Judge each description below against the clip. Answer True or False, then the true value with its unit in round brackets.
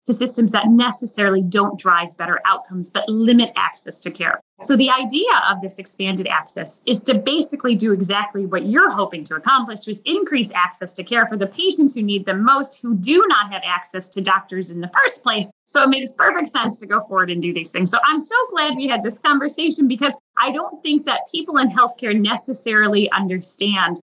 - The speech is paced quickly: True (210 wpm)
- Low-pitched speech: False (220 Hz)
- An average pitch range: False (6.1 semitones)